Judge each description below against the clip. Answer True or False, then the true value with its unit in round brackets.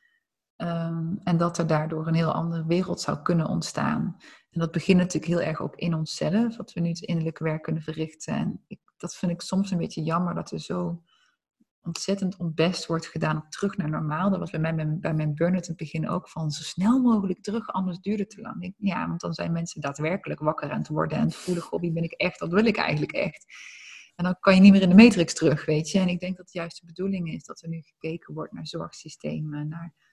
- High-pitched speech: False (170 Hz)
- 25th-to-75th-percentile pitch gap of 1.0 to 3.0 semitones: True (2.6 semitones)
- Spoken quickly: True (245 wpm)